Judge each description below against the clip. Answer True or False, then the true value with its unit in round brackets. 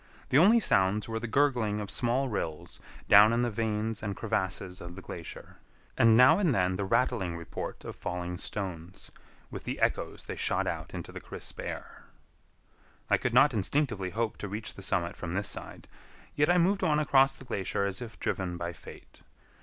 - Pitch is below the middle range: True (105 Hz)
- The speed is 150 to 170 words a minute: False (190 wpm)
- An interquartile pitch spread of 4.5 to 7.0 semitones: True (4.9 semitones)